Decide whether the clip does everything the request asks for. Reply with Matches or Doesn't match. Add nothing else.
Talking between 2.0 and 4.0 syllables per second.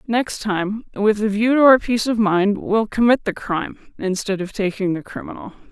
Matches